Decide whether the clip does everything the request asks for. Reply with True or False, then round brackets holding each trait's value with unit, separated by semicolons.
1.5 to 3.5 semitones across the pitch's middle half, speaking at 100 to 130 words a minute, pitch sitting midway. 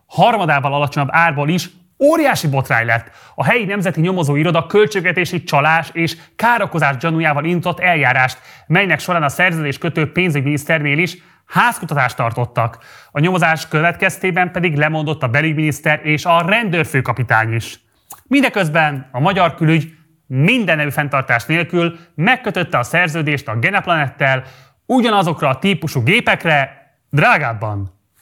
False (4.1 semitones; 120 wpm; 160 Hz)